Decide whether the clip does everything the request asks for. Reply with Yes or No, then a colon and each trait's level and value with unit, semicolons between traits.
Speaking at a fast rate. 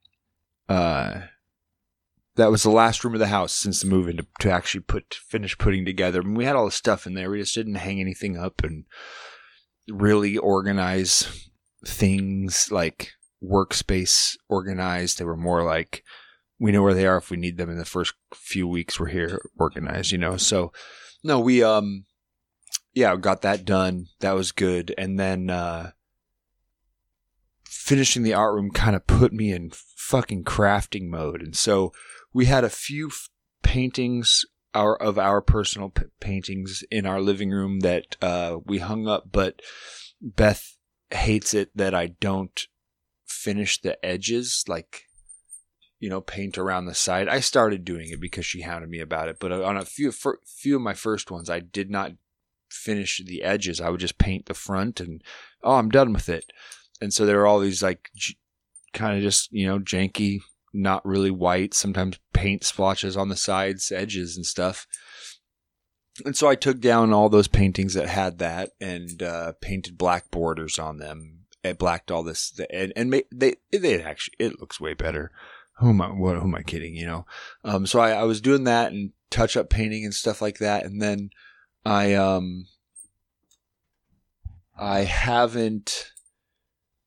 No: average, 175 wpm